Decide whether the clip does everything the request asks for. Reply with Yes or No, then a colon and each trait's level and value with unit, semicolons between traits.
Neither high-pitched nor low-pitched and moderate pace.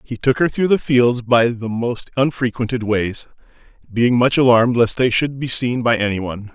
No: low, 120 Hz; average, 195 wpm